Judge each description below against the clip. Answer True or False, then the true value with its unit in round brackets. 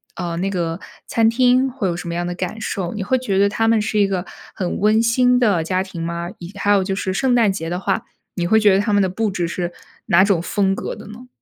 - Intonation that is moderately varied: True (3.7 semitones)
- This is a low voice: False (195 Hz)